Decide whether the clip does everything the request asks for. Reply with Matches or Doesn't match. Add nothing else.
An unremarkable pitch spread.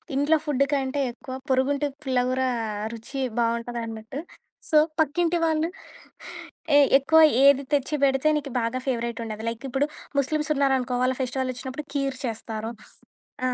Matches